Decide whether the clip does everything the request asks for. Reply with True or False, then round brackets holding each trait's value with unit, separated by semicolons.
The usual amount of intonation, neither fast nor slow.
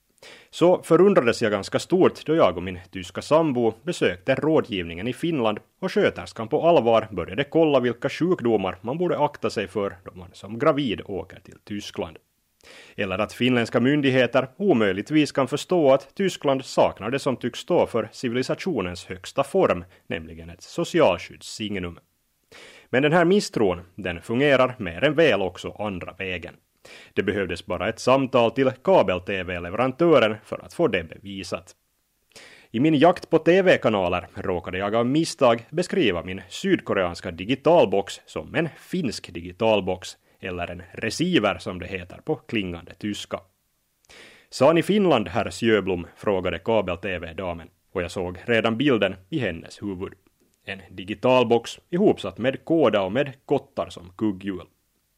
False (6.6 semitones; 140 wpm)